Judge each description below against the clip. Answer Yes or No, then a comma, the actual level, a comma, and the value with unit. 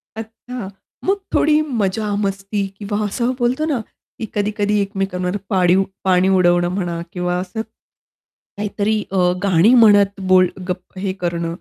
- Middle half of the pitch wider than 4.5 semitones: No, average, 2.9 semitones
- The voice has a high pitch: Yes, high, 200 Hz